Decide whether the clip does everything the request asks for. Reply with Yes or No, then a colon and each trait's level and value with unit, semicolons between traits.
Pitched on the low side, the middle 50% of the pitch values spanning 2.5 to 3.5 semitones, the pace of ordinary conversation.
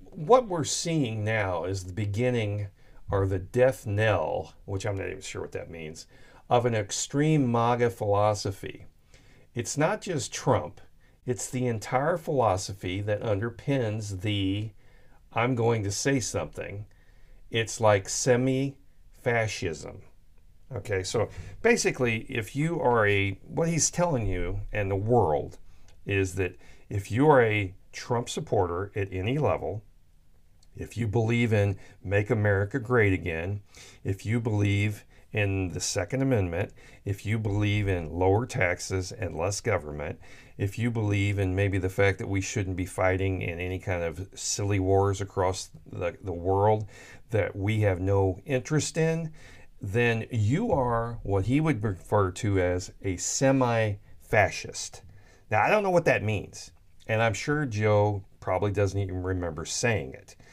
No: low, 105 Hz; average, 4.3 semitones; average, 150 wpm